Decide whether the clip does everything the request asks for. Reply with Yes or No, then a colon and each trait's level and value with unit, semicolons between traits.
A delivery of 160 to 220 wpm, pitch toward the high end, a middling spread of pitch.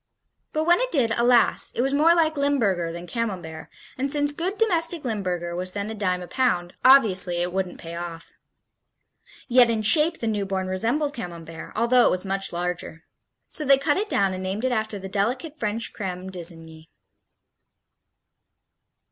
No: average, 170 wpm; high, 210 Hz; wide, 7.3 semitones